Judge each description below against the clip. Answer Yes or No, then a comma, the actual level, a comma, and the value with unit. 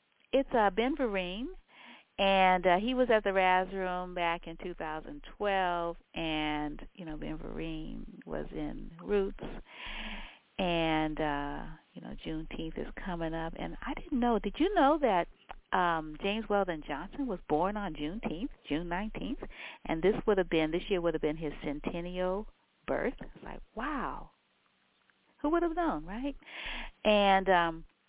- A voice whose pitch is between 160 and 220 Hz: Yes, medium, 185 Hz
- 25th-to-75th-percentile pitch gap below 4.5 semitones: No, average, 5.2 semitones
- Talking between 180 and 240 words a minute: No, average, 160 wpm